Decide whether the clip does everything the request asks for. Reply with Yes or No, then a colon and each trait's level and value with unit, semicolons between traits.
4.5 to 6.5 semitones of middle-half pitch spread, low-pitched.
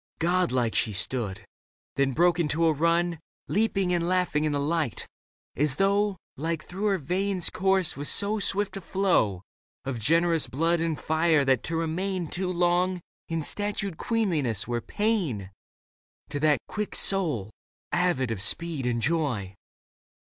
No: average, 5.1 semitones; medium, 165 Hz